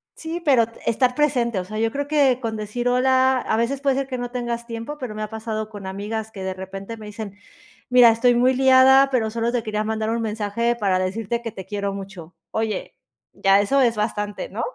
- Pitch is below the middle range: No, high, 230 Hz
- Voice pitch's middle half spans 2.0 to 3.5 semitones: Yes, average, 3.1 semitones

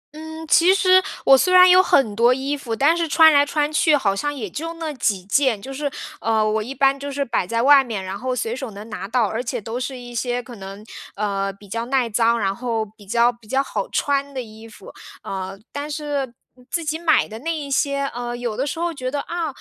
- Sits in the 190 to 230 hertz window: No, very high, 255 Hz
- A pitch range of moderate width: Yes, average, 4.7 semitones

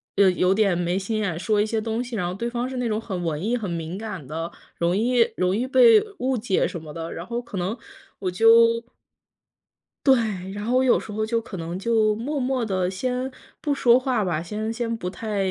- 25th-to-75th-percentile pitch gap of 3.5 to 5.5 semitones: Yes, average, 4.6 semitones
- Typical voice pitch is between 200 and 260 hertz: Yes, high, 215 Hz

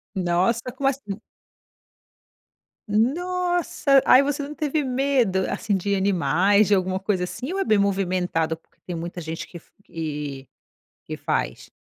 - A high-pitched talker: Yes, high, 200 Hz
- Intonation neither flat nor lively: No, wide, 7.4 semitones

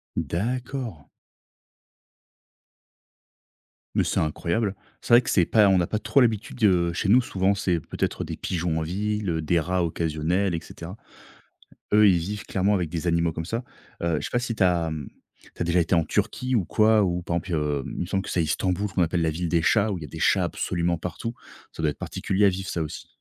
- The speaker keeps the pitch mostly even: No, average, 3.8 semitones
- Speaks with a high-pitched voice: No, very low, 90 Hz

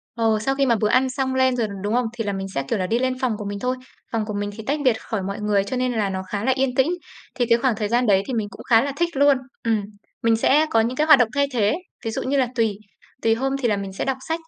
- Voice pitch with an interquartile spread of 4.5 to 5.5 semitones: No, average, 3.8 semitones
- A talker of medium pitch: No, high, 235 Hz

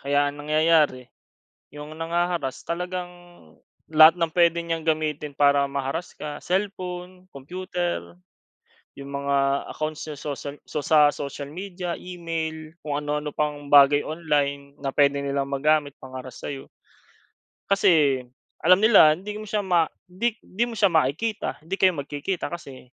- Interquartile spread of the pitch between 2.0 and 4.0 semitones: Yes, average, 3.7 semitones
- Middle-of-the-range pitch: Yes, medium, 155 Hz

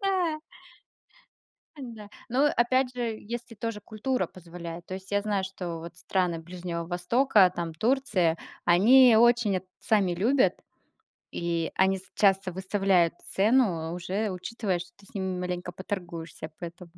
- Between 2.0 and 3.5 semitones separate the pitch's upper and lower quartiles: No, average, 4.6 semitones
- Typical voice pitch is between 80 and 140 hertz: No, high, 190 Hz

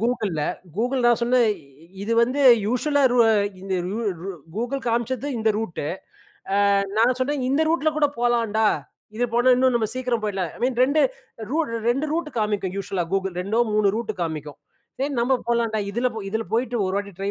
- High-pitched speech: Yes, high, 235 Hz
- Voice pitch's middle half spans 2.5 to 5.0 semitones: Yes, average, 3.6 semitones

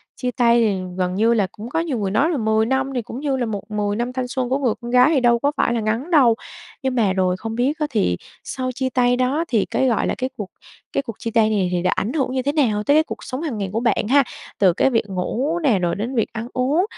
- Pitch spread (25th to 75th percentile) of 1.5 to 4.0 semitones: Yes, average, 3.7 semitones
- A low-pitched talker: No, high, 240 Hz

